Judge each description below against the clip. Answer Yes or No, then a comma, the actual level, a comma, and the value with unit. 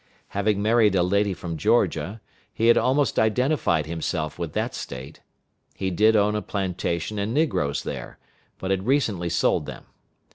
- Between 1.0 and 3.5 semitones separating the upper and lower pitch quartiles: No, average, 4.4 semitones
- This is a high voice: No, low, 100 Hz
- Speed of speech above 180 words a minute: No, average, 155 wpm